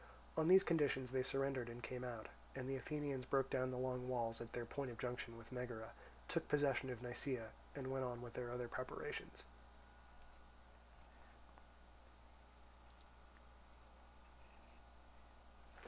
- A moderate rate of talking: No, slow, 130 wpm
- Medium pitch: No, low, 125 Hz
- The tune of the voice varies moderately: No, narrow, 1.9 semitones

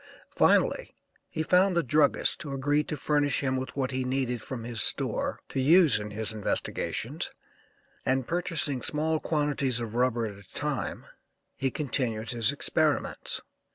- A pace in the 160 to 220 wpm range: No, average, 150 wpm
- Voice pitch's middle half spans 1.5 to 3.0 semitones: No, average, 4.1 semitones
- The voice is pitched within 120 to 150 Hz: Yes, low, 135 Hz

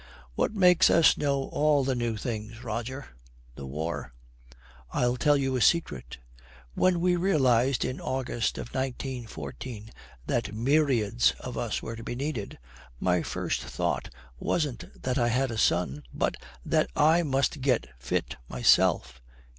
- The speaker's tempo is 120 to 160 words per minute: Yes, average, 145 wpm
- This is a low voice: Yes, low, 125 Hz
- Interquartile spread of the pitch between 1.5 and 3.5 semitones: No, average, 4.7 semitones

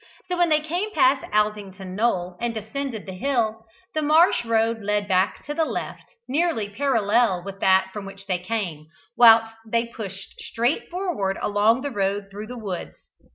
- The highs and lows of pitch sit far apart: No, average, 4.8 semitones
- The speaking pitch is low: No, high, 220 Hz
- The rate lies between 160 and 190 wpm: Yes, average, 170 wpm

